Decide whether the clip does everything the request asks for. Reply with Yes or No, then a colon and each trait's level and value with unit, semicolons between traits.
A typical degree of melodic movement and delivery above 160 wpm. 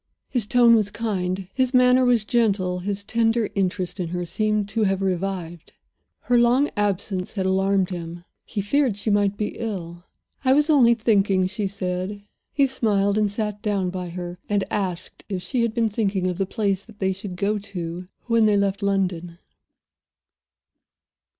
Yes: average, 3.1 semitones; average, 170 wpm